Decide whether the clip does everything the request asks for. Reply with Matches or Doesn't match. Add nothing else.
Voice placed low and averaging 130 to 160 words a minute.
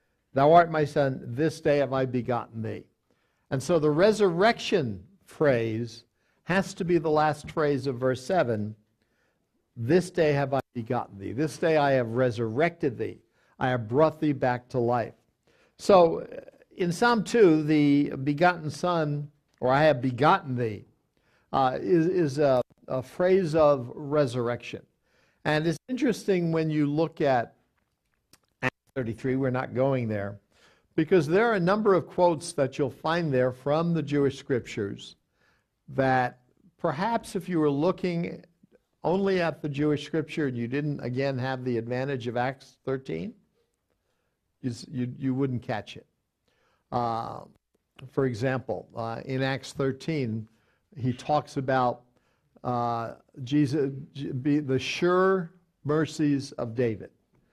Doesn't match